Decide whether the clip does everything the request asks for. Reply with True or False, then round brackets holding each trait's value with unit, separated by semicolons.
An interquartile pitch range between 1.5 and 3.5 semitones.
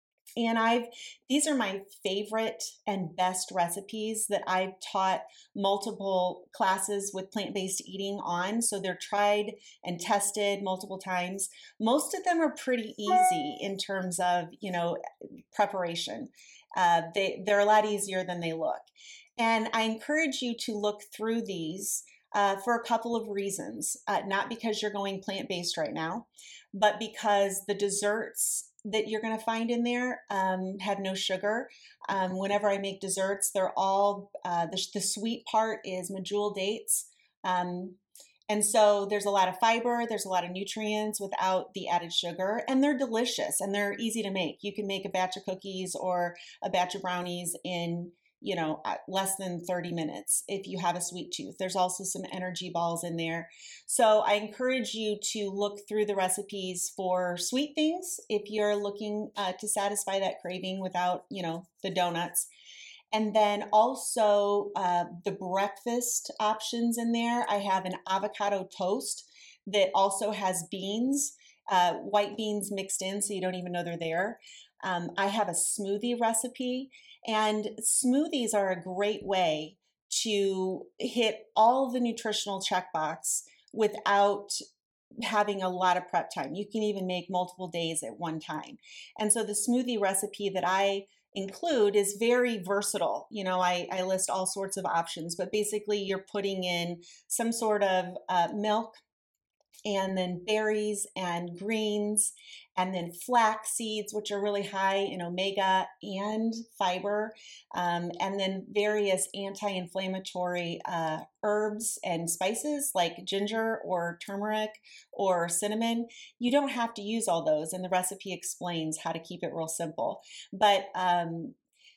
True (2.8 semitones)